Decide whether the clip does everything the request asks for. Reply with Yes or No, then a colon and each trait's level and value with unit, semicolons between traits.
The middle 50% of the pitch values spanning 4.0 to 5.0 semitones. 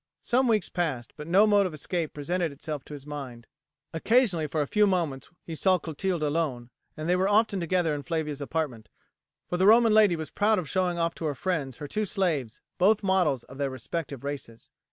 Yes: average, 4.7 semitones